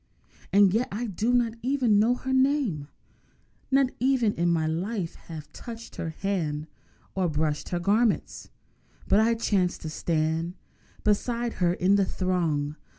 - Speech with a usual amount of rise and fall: No, wide, 5.9 semitones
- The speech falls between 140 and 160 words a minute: Yes, average, 150 wpm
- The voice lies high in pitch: Yes, high, 195 Hz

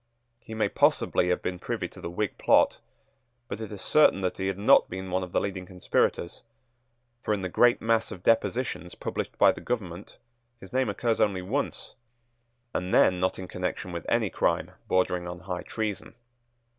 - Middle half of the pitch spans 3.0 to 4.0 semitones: Yes, average, 3.3 semitones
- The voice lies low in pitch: Yes, very low, 95 Hz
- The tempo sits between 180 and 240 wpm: Yes, average, 185 wpm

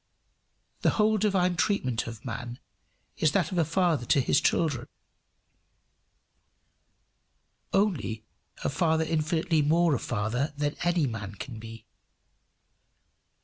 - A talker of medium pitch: Yes, medium, 150 Hz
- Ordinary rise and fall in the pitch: No, wide, 6.3 semitones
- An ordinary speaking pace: No, slow, 115 wpm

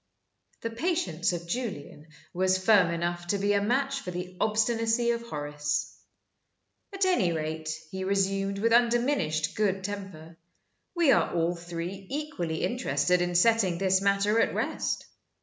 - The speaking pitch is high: Yes, high, 195 Hz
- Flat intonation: No, average, 5.0 semitones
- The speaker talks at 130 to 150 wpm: Yes, average, 145 wpm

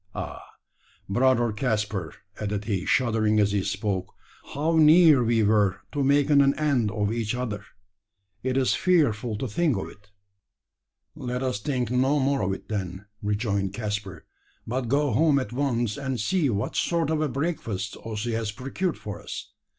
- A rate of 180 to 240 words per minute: No, average, 160 wpm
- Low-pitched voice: Yes, low, 115 Hz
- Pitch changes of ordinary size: Yes, average, 5.0 semitones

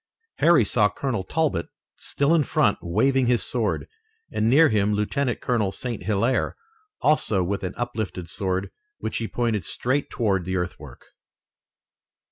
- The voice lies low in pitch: Yes, low, 110 Hz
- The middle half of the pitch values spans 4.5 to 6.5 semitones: Yes, average, 5.0 semitones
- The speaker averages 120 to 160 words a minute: Yes, average, 140 wpm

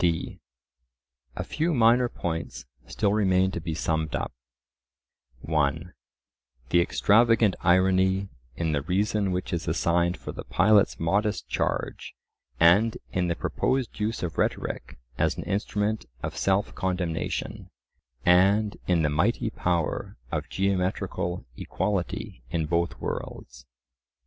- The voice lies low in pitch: Yes, very low, 90 Hz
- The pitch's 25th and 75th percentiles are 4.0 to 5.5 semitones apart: No, average, 3.4 semitones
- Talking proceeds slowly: Yes, slow, 125 wpm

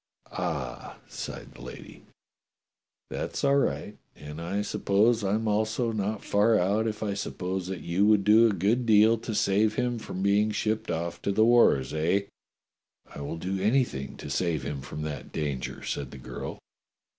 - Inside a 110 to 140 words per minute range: No, average, 175 wpm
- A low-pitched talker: Yes, low, 100 Hz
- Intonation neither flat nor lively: Yes, average, 4.5 semitones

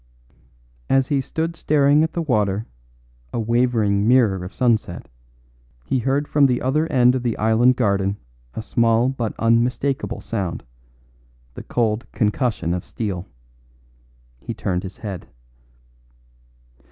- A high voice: No, low, 115 Hz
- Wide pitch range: No, average, 4.2 semitones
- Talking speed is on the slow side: Yes, slow, 130 wpm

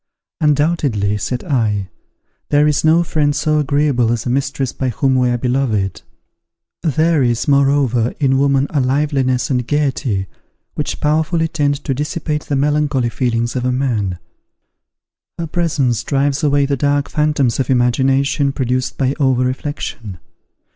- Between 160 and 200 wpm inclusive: No, average, 145 wpm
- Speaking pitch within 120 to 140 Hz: Yes, low, 135 Hz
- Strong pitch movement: No, average, 3.0 semitones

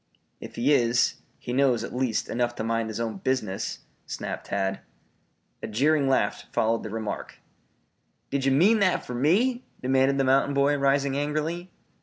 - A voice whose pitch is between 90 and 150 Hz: Yes, low, 135 Hz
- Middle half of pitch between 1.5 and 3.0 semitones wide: No, average, 3.7 semitones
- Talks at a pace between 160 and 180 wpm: Yes, average, 165 wpm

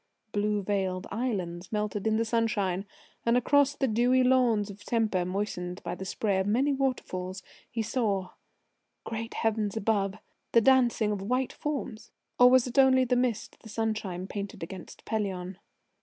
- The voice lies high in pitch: Yes, high, 215 Hz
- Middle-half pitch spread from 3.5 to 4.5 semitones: Yes, average, 3.9 semitones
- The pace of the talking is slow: No, average, 155 wpm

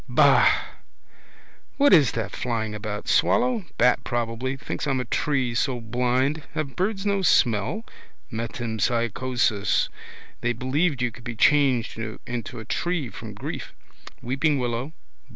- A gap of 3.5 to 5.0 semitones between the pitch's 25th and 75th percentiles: Yes, average, 3.9 semitones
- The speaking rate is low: Yes, slow, 130 wpm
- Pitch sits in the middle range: No, low, 125 Hz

